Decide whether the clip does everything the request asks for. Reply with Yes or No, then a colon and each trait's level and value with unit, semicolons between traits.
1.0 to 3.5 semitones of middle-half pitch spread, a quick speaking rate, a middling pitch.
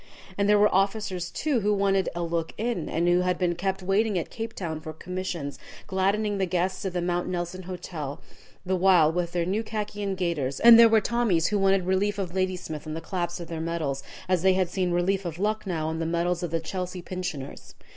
Yes: narrow, 2.4 semitones; fast, 220 wpm; medium, 180 Hz